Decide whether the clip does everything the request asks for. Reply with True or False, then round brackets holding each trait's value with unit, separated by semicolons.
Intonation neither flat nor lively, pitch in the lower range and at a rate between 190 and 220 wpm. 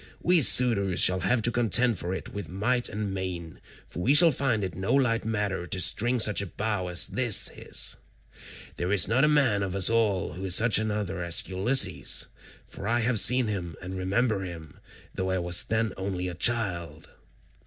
True (4.2 semitones; 100 Hz; 195 wpm)